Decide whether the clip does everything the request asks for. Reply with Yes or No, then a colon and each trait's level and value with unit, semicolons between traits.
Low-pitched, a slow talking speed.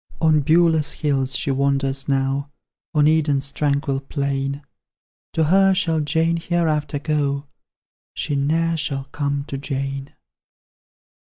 No: medium, 145 Hz; slow, 115 wpm